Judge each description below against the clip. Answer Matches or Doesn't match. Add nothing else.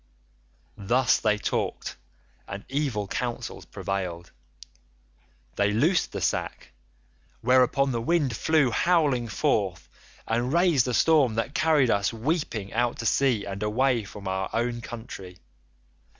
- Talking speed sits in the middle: Doesn't match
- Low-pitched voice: Matches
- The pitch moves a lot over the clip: Doesn't match